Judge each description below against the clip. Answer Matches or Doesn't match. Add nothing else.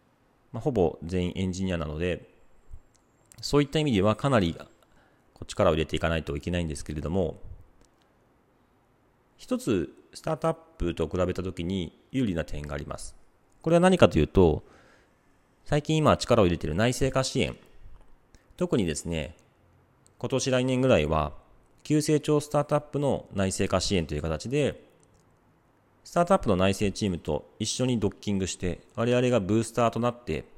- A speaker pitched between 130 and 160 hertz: Doesn't match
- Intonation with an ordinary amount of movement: Doesn't match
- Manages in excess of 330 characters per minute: Doesn't match